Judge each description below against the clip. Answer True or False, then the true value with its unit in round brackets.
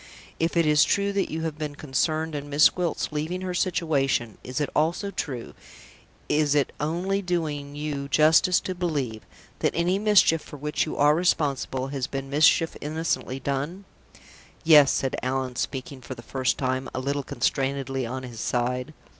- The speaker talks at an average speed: True (170 wpm)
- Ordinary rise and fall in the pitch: True (3.5 semitones)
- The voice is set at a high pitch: False (150 Hz)